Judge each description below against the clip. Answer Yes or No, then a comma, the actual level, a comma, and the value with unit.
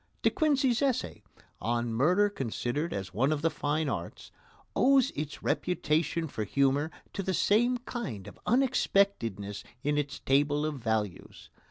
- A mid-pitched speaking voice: Yes, medium, 150 Hz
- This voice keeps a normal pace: Yes, average, 145 wpm